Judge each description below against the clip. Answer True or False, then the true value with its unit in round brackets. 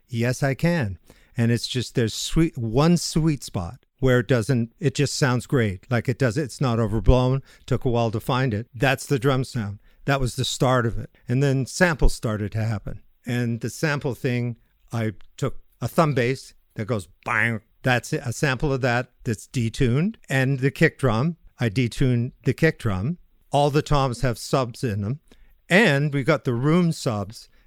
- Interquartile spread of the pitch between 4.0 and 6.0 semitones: False (3.4 semitones)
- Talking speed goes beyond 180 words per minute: True (190 wpm)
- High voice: False (125 Hz)